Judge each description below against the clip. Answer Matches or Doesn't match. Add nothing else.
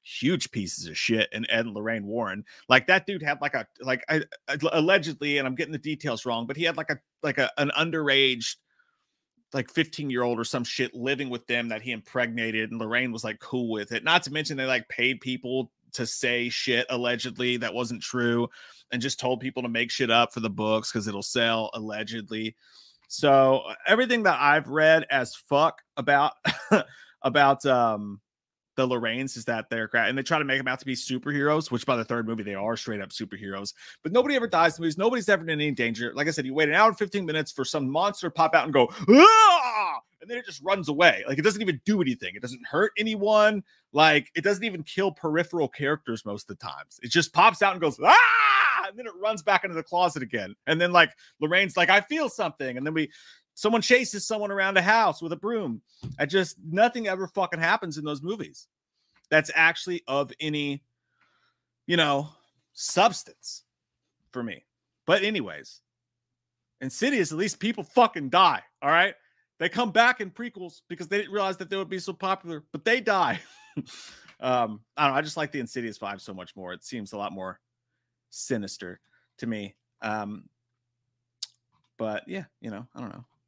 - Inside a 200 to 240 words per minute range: Matches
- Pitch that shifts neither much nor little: Doesn't match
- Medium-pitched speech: Matches